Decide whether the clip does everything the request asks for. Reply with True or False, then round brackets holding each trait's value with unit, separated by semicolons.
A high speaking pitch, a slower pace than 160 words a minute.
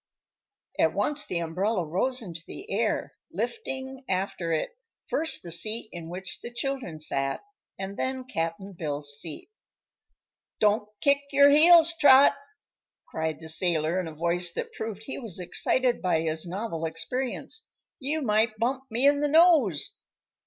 True (210 Hz; 150 wpm)